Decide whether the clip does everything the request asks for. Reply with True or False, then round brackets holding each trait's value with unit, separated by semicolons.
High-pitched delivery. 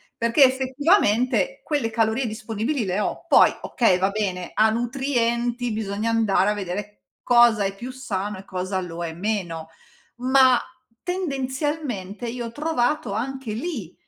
True (230 Hz)